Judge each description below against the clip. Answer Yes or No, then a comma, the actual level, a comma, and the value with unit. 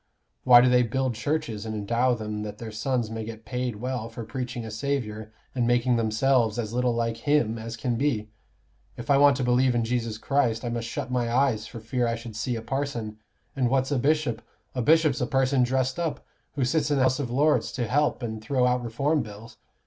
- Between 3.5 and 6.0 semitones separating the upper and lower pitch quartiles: No, average, 2.7 semitones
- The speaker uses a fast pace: Yes, fast, 220 wpm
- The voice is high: No, low, 120 Hz